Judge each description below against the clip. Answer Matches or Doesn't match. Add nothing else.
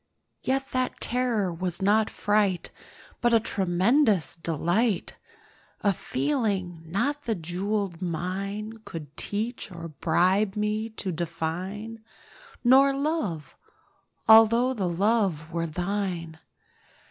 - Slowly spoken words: Matches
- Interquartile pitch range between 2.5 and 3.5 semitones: Doesn't match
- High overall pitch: Matches